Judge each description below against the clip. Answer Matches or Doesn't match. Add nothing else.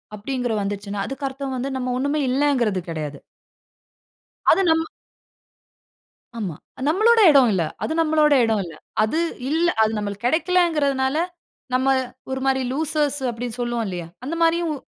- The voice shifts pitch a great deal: Matches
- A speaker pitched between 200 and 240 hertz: Doesn't match